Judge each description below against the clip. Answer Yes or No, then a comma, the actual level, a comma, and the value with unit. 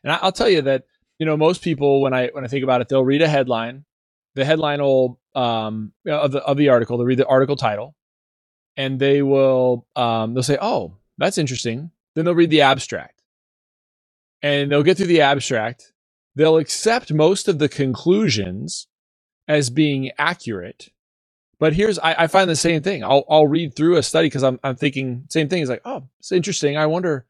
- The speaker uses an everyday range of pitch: Yes, average, 3.8 semitones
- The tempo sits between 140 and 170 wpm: No, fast, 205 wpm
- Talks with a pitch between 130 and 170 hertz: Yes, medium, 140 Hz